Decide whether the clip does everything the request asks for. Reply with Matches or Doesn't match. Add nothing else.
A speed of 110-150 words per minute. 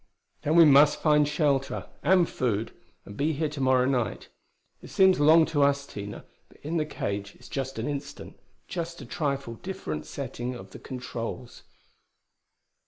Doesn't match